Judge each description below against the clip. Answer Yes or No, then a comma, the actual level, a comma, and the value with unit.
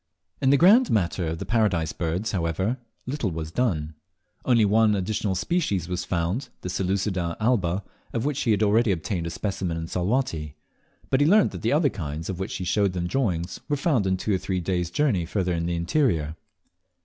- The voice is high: No, very low, 95 Hz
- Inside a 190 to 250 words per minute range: Yes, average, 195 wpm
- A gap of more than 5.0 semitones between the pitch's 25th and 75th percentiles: Yes, wide, 5.5 semitones